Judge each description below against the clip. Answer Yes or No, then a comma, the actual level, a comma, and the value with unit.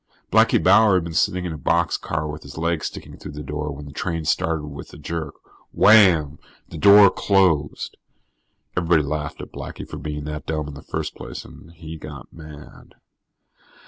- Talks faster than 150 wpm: Yes, average, 180 wpm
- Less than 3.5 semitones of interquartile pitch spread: Yes, narrow, 2.4 semitones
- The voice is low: Yes, very low, 80 Hz